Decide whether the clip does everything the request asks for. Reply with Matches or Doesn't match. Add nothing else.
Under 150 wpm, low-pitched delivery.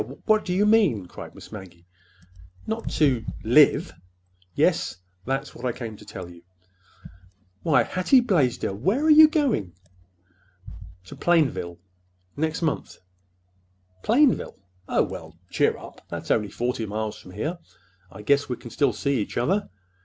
Matches